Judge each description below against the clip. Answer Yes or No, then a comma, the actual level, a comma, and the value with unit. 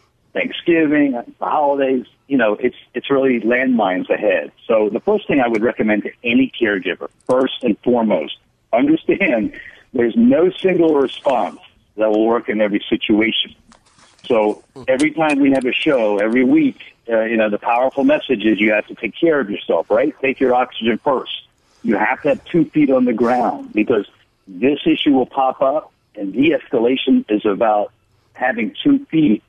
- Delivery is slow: No, average, 170 wpm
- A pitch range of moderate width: No, wide, 8.8 semitones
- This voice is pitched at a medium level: No, low, 130 Hz